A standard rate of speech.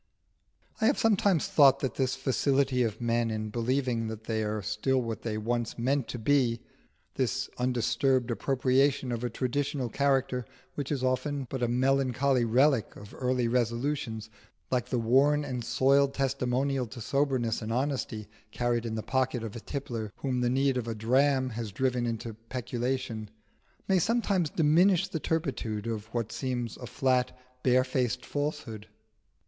Yes: average, 155 wpm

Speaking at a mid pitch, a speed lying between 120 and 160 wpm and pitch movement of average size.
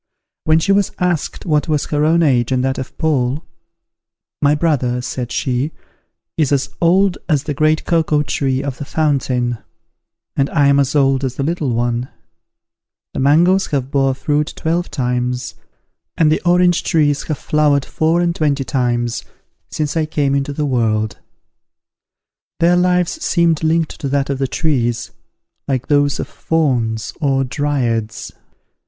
Yes: medium, 145 Hz; average, 155 wpm; average, 3.5 semitones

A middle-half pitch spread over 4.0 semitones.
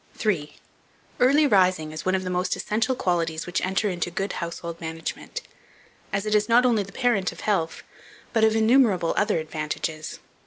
Yes: average, 4.7 semitones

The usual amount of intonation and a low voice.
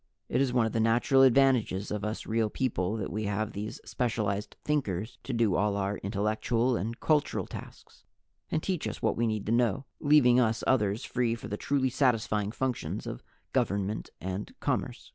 Yes: average, 3.4 semitones; low, 115 Hz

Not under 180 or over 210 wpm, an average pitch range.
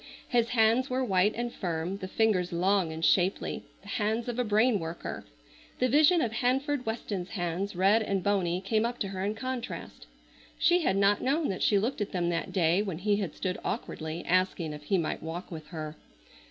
Yes: average, 200 wpm; average, 4.6 semitones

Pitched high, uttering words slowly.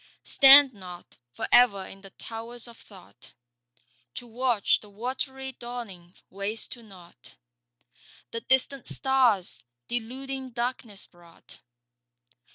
Yes: high, 235 Hz; slow, 110 wpm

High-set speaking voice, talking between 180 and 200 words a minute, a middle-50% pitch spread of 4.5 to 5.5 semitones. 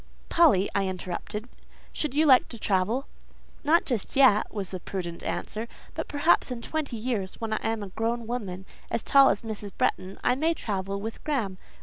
Yes: high, 225 Hz; average, 185 wpm; average, 4.9 semitones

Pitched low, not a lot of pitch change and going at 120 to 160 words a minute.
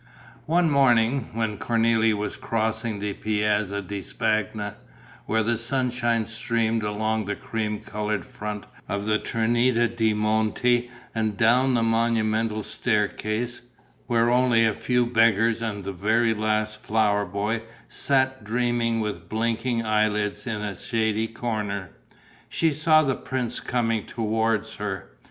Yes: low, 110 Hz; narrow, 1.8 semitones; slow, 135 wpm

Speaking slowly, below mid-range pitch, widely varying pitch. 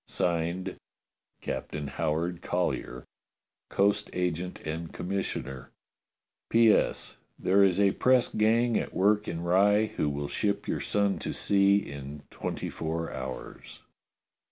No: slow, 120 wpm; very low, 90 Hz; average, 4.4 semitones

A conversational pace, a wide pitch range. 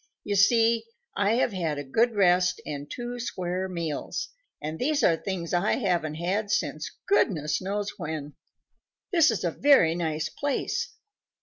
Yes: average, 150 wpm; wide, 5.9 semitones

